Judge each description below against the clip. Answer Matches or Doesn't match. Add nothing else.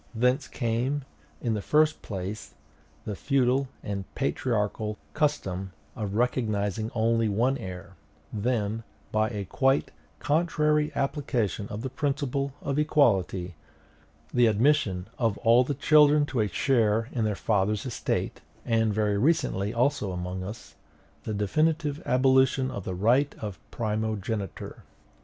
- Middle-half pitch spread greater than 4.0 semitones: Matches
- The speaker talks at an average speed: Doesn't match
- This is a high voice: Doesn't match